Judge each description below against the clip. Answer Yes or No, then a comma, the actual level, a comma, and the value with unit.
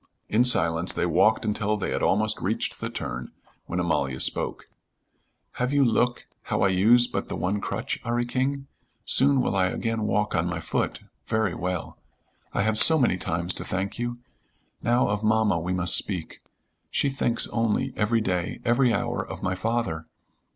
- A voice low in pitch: Yes, low, 105 Hz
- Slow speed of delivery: No, average, 175 wpm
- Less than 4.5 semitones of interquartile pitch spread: No, average, 4.8 semitones